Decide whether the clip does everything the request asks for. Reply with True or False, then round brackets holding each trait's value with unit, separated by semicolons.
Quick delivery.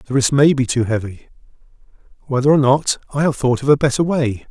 True (215 wpm)